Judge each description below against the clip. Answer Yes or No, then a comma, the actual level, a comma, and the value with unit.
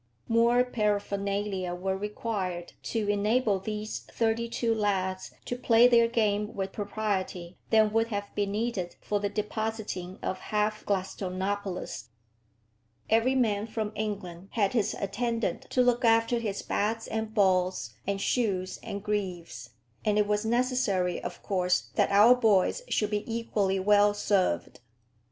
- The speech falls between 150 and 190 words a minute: No, average, 140 wpm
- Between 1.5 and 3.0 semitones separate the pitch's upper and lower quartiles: Yes, average, 2.7 semitones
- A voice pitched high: Yes, high, 210 Hz